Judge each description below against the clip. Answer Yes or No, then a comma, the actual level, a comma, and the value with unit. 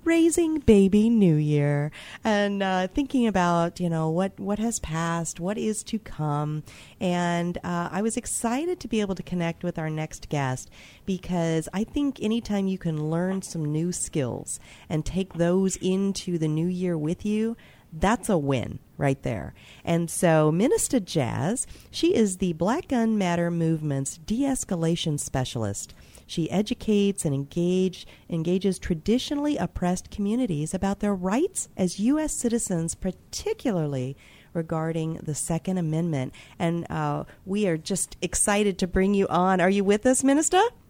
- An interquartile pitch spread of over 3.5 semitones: Yes, average, 4.6 semitones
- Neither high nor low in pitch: Yes, medium, 180 Hz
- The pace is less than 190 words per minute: Yes, average, 150 wpm